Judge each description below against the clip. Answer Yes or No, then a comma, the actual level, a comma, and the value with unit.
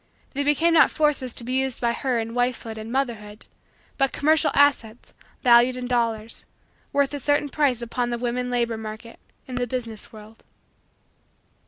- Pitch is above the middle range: Yes, high, 245 Hz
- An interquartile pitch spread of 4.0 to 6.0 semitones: No, average, 2.9 semitones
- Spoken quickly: No, average, 165 wpm